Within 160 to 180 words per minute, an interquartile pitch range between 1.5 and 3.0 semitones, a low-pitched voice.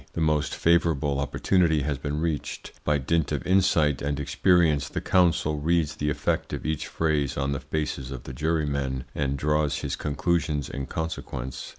Yes: average, 170 wpm; narrow, 2.5 semitones; very low, 75 Hz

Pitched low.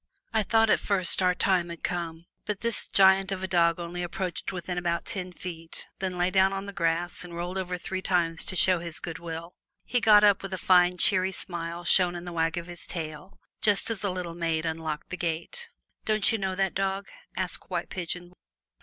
No: medium, 180 Hz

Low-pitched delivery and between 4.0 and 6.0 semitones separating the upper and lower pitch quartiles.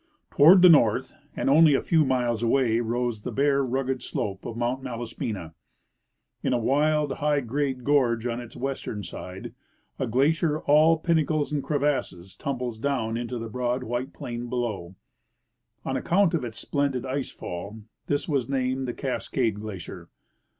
No: low, 125 Hz; average, 3.5 semitones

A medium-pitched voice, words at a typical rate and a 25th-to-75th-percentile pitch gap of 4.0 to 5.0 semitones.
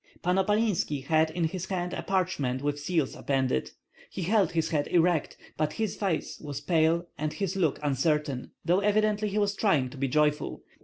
Yes: medium, 165 Hz; average, 185 wpm; average, 4.7 semitones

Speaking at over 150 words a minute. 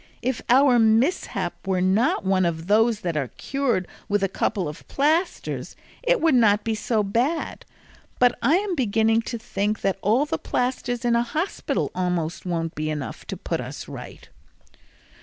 Yes: average, 165 wpm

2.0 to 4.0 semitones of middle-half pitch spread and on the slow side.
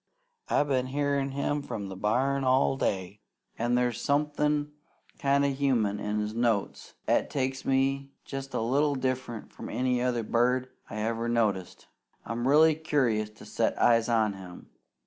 No: average, 3.6 semitones; average, 160 wpm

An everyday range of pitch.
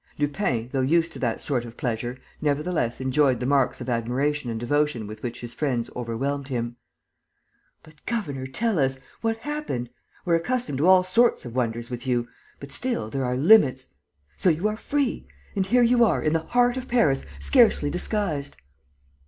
No: wide, 7.5 semitones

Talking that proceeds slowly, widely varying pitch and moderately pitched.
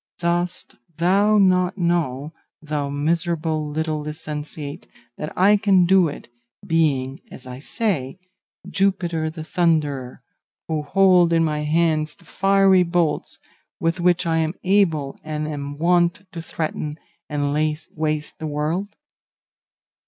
No: slow, 130 wpm; average, 2.9 semitones; medium, 160 Hz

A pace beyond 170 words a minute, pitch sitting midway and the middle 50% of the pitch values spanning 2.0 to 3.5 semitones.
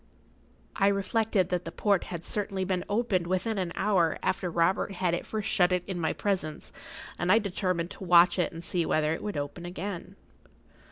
Yes: average, 190 wpm; medium, 180 Hz; narrow, 2.4 semitones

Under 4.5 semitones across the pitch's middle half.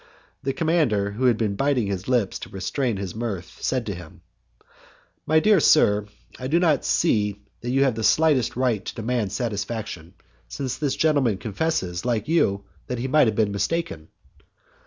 No: average, 5.3 semitones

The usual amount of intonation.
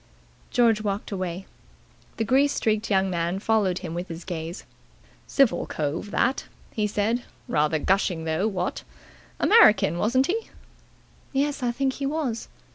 No: wide, 5.8 semitones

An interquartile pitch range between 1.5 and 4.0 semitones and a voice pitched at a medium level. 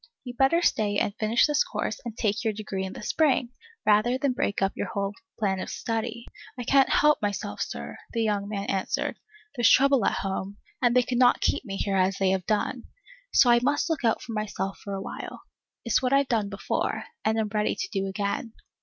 No: average, 3.7 semitones; high, 220 Hz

